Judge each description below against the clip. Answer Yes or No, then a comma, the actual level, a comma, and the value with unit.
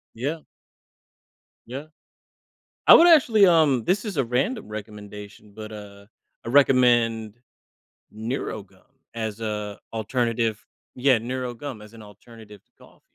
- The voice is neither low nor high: No, low, 115 Hz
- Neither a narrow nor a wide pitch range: Yes, average, 4.0 semitones